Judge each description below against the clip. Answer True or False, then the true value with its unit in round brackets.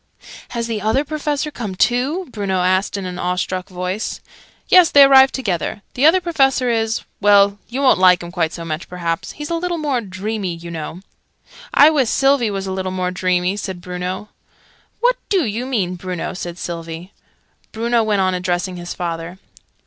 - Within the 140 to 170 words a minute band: False (180 wpm)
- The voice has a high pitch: True (195 Hz)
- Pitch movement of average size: False (6.2 semitones)